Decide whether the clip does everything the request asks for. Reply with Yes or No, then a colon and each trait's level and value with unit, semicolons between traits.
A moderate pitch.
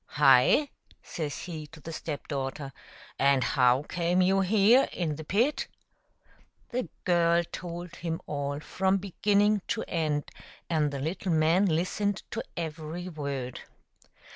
Yes: medium, 165 Hz